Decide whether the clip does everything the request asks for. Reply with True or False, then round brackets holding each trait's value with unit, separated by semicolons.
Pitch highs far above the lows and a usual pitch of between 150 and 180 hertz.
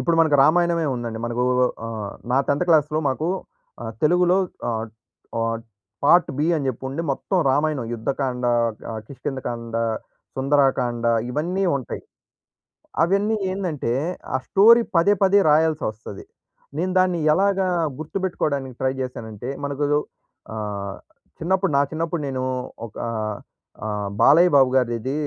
False (6.2 semitones; 140 Hz)